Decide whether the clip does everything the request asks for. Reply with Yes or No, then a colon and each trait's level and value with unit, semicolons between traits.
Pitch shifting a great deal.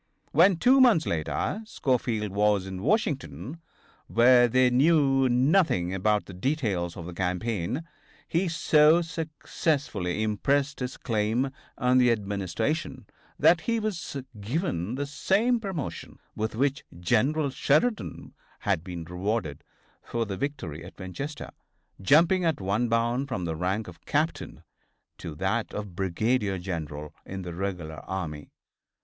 Yes: wide, 8.0 semitones